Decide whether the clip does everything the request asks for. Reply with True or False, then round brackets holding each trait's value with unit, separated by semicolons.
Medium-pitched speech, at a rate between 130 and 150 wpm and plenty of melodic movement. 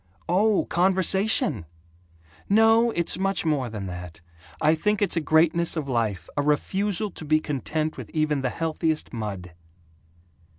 True (160 Hz; 140 wpm; 6.4 semitones)